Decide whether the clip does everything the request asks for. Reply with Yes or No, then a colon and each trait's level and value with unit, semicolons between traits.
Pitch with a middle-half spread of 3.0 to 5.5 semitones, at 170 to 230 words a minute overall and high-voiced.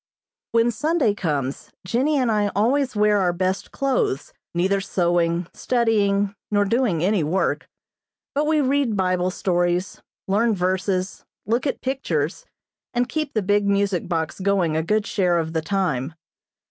No: average, 4.7 semitones; average, 145 wpm; high, 200 Hz